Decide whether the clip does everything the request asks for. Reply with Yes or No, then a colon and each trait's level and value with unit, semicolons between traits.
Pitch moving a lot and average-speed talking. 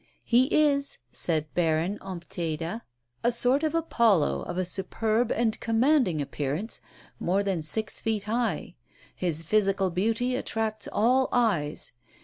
No: wide, 5.7 semitones; slow, 130 wpm